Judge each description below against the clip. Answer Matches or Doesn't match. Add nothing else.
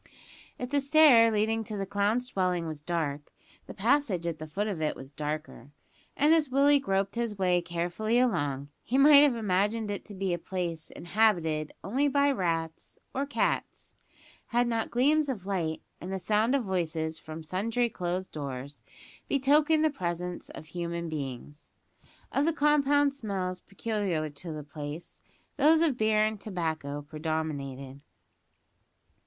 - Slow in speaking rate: Doesn't match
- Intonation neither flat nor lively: Doesn't match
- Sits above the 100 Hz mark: Matches